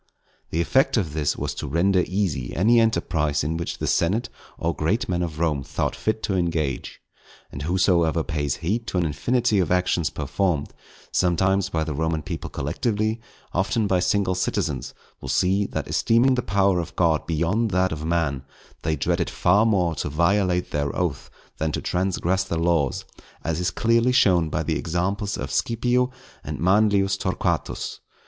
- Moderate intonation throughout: Yes, average, 4.0 semitones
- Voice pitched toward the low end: Yes, very low, 90 Hz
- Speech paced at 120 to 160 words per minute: No, average, 170 wpm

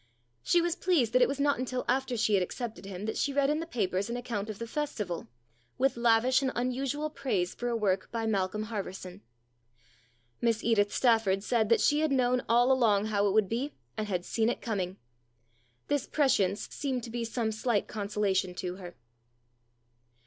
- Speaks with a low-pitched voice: No, high, 230 Hz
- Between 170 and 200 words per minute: Yes, average, 190 wpm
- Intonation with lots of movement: No, average, 4.2 semitones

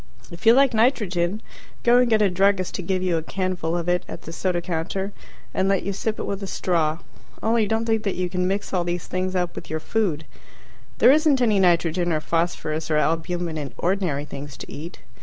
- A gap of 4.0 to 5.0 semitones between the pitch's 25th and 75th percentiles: No, average, 3.3 semitones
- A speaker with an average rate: No, fast, 215 wpm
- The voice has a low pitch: No, medium, 185 Hz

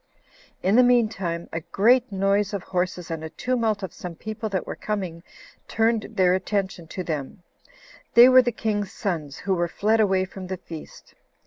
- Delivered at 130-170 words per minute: No, average, 185 wpm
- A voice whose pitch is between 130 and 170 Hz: No, high, 195 Hz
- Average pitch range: Yes, average, 3.6 semitones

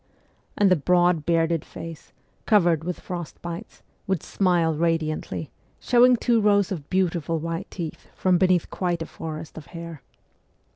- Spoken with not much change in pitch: Yes, narrow, 2.2 semitones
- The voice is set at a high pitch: No, medium, 170 Hz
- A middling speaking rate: Yes, average, 145 wpm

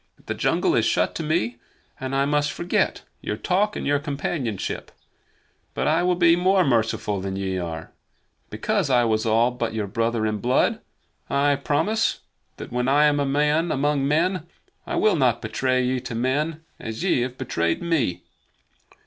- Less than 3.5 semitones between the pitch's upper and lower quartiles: No, average, 5.2 semitones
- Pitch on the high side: No, low, 135 Hz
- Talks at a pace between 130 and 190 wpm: Yes, average, 175 wpm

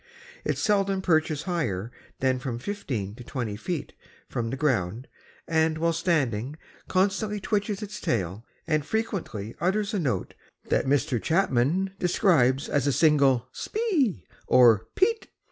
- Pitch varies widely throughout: Yes, wide, 7.8 semitones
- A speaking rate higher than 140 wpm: No, slow, 135 wpm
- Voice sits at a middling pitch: Yes, medium, 150 Hz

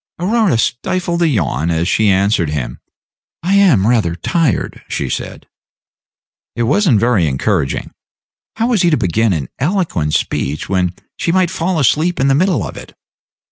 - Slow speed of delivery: No, average, 165 wpm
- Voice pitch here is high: No, low, 120 Hz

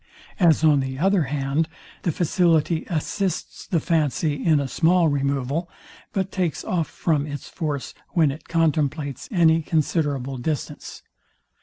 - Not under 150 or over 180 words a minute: No, slow, 135 wpm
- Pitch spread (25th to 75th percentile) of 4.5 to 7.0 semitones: No, average, 3.0 semitones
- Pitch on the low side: No, medium, 155 Hz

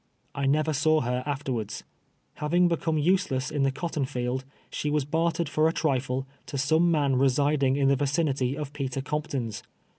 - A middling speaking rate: Yes, average, 170 wpm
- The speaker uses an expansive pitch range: No, average, 2.7 semitones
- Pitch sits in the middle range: Yes, medium, 145 Hz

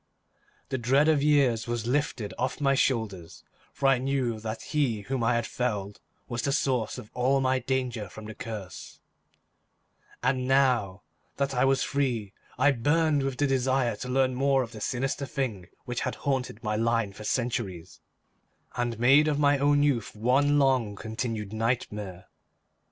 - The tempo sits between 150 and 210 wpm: Yes, average, 165 wpm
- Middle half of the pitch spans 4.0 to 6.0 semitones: No, average, 3.5 semitones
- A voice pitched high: No, low, 125 Hz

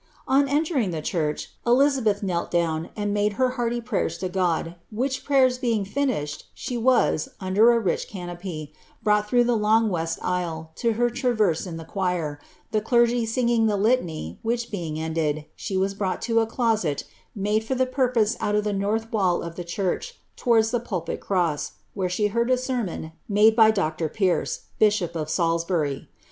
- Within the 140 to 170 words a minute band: No, average, 180 wpm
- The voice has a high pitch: Yes, high, 210 Hz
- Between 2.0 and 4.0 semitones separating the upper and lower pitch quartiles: No, wide, 5.4 semitones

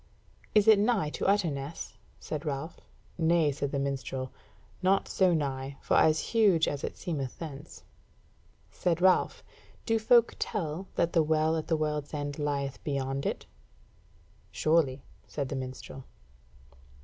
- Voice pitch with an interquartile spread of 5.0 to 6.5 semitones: No, average, 3.8 semitones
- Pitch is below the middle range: No, medium, 155 Hz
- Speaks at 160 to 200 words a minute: No, average, 140 wpm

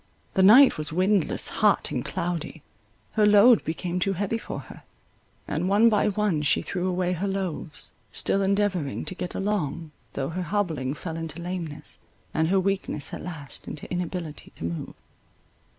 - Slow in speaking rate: No, average, 165 wpm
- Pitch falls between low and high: Yes, medium, 180 Hz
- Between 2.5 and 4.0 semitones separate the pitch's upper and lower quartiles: Yes, average, 3.6 semitones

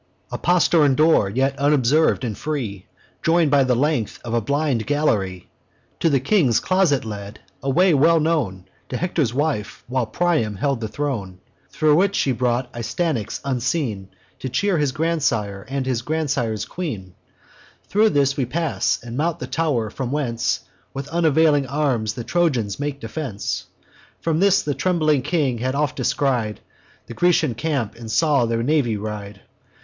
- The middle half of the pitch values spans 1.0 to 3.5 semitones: No, average, 5.3 semitones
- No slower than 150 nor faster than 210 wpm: Yes, average, 160 wpm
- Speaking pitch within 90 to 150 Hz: Yes, low, 135 Hz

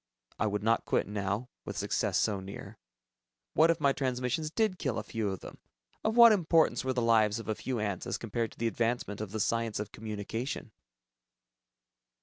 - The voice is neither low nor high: No, low, 115 Hz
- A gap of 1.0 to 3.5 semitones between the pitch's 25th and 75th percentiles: No, average, 4.1 semitones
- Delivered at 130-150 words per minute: No, average, 190 wpm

